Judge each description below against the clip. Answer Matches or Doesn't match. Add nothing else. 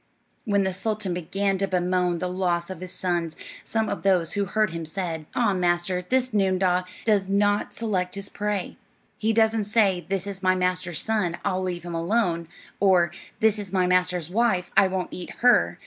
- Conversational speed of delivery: Matches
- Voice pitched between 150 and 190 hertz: Matches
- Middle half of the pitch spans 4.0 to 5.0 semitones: Doesn't match